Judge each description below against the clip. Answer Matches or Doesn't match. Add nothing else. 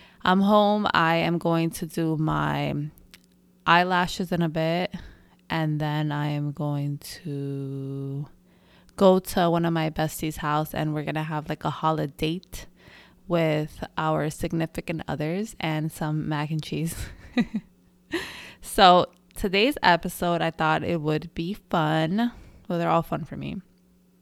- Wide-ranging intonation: Doesn't match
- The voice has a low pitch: Doesn't match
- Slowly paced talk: Doesn't match